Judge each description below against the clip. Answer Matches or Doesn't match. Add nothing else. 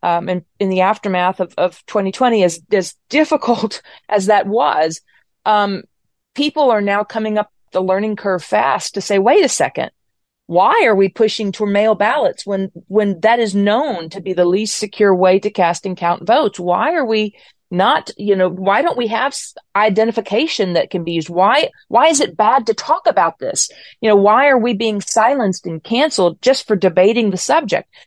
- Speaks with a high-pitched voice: Matches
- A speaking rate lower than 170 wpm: Doesn't match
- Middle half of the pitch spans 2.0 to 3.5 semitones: Matches